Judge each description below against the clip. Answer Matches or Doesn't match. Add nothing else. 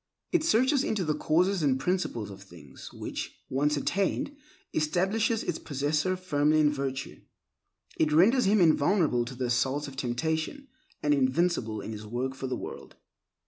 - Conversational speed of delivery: Matches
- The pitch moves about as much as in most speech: Doesn't match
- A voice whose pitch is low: Doesn't match